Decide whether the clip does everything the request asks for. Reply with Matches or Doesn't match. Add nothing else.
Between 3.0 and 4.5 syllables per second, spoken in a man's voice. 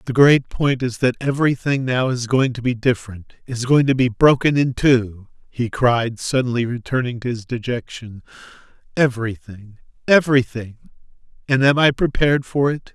Doesn't match